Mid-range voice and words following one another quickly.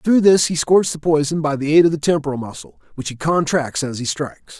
Yes: medium, 150 Hz; fast, 250 wpm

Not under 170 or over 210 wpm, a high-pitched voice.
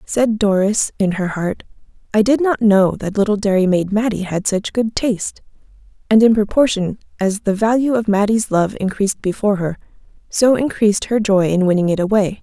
Yes: average, 185 wpm; high, 205 Hz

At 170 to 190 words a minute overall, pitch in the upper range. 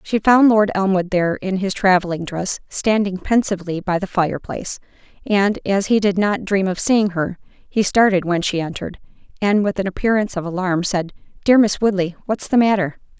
Yes: average, 185 wpm; high, 195 Hz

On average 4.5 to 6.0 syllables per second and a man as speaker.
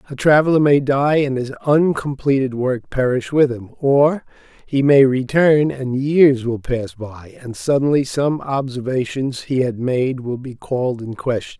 No: 4.3 syllables/s; male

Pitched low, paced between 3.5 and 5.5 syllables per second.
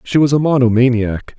Yes: low, 125 Hz; 5.4 syllables/s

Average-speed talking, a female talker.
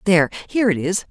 No: fast, 215 wpm; female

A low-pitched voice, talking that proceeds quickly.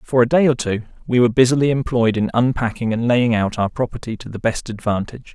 Yes: low, 120 Hz; fast, 225 wpm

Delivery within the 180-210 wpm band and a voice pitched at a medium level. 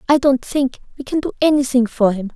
No: fast, 205 wpm; very high, 265 Hz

